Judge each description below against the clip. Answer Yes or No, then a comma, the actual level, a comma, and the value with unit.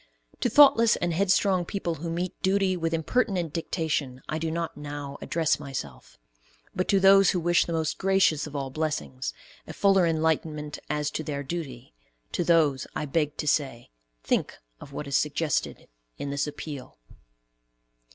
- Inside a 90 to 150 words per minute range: No, average, 160 wpm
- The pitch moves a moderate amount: Yes, average, 3.4 semitones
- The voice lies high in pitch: No, medium, 160 Hz